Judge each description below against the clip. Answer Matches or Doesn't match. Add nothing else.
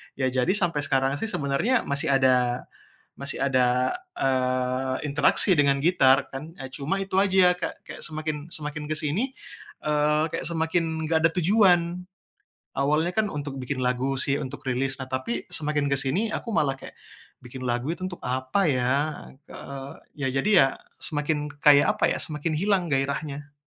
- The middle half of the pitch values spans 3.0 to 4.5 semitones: Matches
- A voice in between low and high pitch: Matches